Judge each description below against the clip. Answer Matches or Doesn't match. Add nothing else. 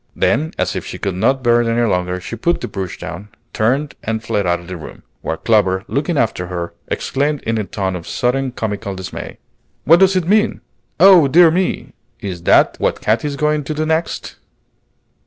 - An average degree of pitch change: Doesn't match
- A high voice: Doesn't match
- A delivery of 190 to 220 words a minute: Matches